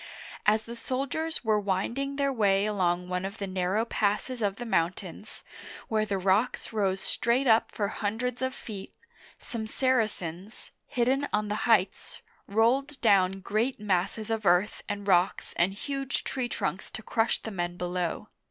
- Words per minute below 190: Yes, average, 160 wpm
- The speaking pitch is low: No, high, 210 Hz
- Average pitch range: Yes, average, 3.7 semitones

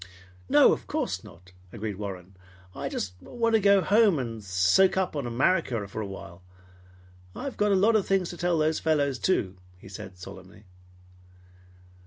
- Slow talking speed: No, average, 165 wpm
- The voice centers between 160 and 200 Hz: No, low, 130 Hz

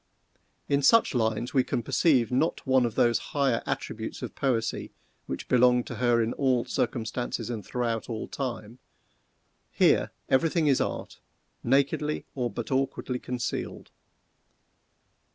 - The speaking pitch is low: Yes, low, 125 Hz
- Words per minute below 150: Yes, slow, 135 wpm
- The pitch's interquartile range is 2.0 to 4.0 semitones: Yes, narrow, 2.4 semitones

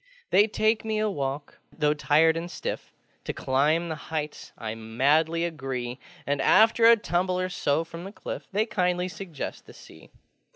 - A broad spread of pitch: No, average, 4.5 semitones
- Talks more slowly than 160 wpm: No, average, 170 wpm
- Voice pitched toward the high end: No, medium, 165 Hz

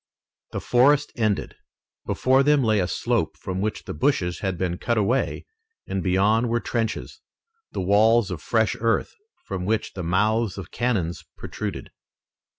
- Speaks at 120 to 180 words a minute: Yes, average, 155 wpm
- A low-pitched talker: Yes, low, 110 Hz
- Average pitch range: Yes, average, 4.0 semitones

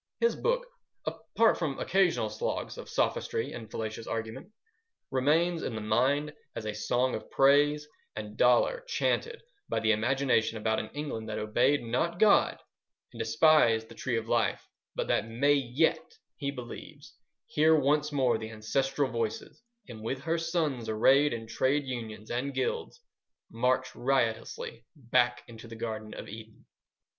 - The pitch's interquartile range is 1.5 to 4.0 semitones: No, average, 5.1 semitones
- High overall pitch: No, low, 130 Hz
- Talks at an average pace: Yes, average, 150 wpm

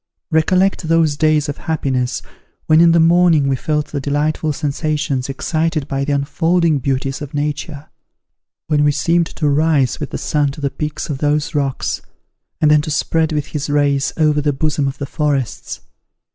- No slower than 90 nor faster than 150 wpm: No, average, 175 wpm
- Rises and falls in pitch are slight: Yes, narrow, 2.0 semitones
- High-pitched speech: No, medium, 150 Hz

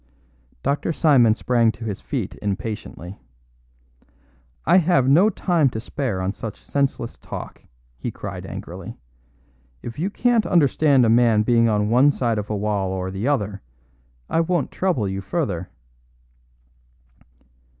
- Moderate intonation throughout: No, wide, 5.8 semitones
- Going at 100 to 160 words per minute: Yes, average, 140 wpm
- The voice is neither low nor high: No, low, 120 Hz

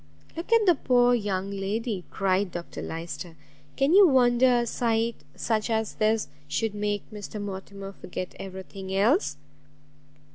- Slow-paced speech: No, average, 145 wpm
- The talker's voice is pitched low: No, high, 215 Hz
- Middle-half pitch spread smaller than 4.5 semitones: Yes, average, 3.9 semitones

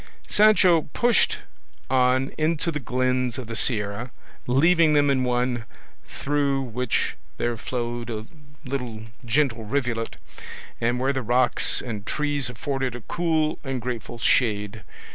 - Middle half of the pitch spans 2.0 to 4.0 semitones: Yes, average, 3.3 semitones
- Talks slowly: Yes, slow, 130 wpm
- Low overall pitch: Yes, low, 125 Hz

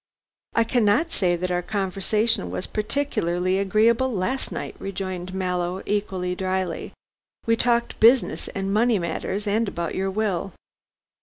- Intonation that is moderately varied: Yes, average, 3.5 semitones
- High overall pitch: Yes, high, 195 Hz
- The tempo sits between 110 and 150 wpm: Yes, slow, 135 wpm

